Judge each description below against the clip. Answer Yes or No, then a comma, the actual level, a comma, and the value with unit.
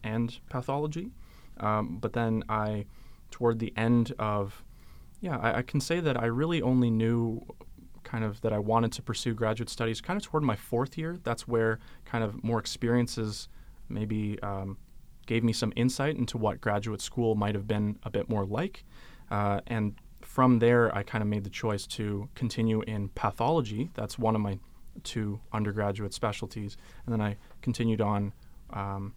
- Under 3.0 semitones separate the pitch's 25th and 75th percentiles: Yes, narrow, 2.4 semitones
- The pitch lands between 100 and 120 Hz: Yes, low, 110 Hz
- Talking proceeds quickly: No, average, 175 wpm